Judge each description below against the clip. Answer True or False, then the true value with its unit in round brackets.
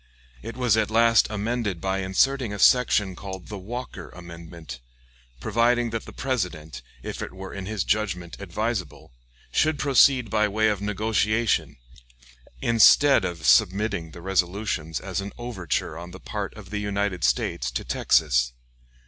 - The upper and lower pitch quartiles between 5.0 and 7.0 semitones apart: False (4.4 semitones)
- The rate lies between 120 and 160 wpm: True (150 wpm)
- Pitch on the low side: True (100 Hz)